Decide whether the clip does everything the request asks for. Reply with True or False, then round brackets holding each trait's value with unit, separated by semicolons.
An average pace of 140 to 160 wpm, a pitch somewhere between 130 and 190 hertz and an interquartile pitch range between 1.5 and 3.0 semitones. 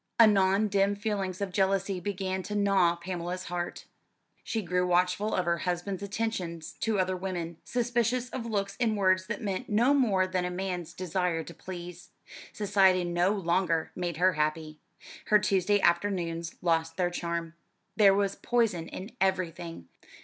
True (155 wpm; 185 Hz; 2.7 semitones)